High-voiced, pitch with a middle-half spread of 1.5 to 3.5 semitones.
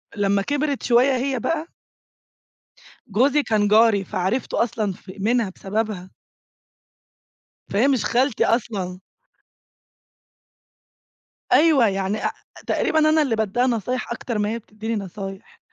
No: high, 225 Hz; average, 4.1 semitones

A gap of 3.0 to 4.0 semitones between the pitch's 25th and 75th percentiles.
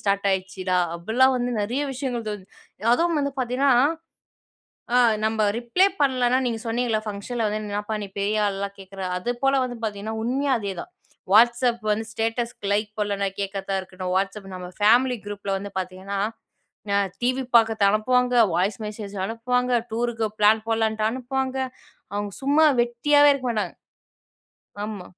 Yes: average, 3.7 semitones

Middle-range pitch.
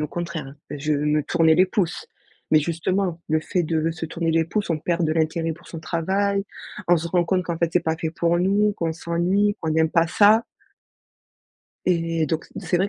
Yes: medium, 165 Hz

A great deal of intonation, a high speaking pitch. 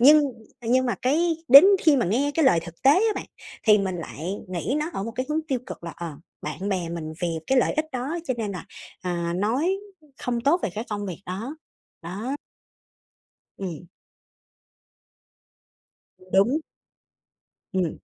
Yes: wide, 7.5 semitones; high, 225 Hz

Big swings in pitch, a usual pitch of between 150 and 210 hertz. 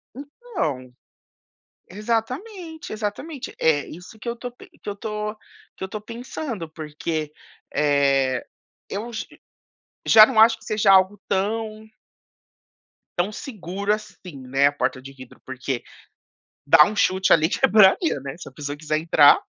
Yes: wide, 6.8 semitones; high, 200 Hz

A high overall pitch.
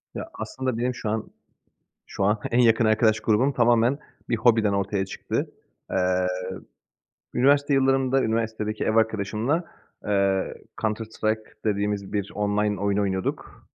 No: low, 110 Hz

